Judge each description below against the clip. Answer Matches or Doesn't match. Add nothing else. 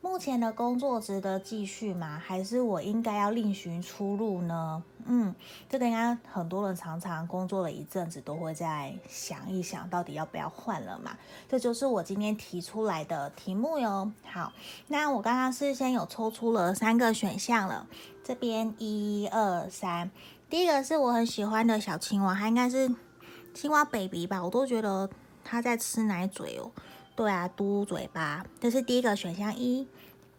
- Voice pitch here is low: Doesn't match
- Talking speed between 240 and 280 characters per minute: Matches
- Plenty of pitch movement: Doesn't match